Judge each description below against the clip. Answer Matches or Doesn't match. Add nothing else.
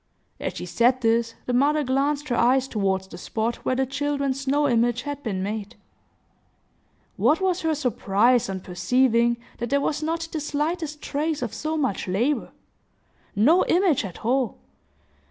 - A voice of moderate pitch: Doesn't match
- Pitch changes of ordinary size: Matches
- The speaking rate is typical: Matches